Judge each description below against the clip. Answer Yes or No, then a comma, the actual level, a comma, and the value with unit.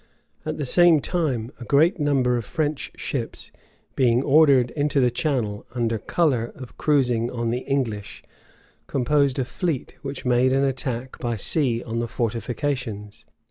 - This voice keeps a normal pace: Yes, average, 150 wpm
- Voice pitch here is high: No, low, 130 Hz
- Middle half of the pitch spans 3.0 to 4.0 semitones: Yes, average, 3.5 semitones